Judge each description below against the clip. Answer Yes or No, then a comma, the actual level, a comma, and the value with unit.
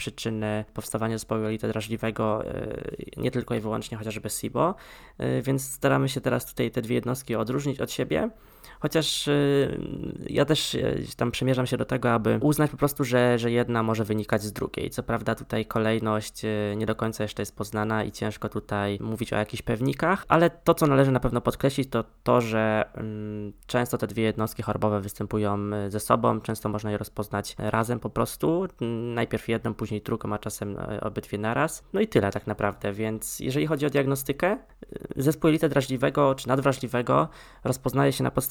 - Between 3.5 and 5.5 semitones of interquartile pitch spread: Yes, average, 4.0 semitones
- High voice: No, low, 115 Hz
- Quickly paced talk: Yes, fast, 170 wpm